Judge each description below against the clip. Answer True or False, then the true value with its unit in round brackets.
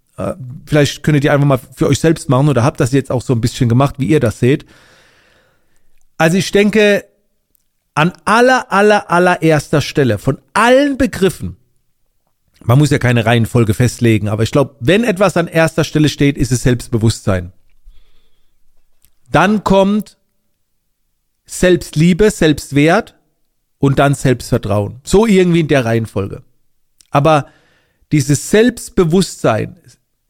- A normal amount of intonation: False (5.8 semitones)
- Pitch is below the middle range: False (145 Hz)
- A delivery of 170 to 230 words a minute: False (130 wpm)